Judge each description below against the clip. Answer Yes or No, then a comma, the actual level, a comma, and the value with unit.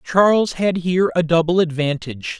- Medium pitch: Yes, medium, 170 Hz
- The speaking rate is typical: Yes, average, 150 wpm